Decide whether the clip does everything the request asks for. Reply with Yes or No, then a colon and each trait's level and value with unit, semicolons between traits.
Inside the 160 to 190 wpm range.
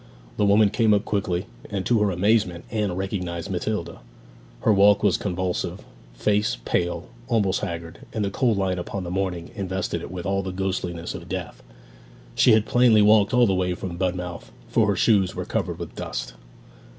Yes: average, 180 wpm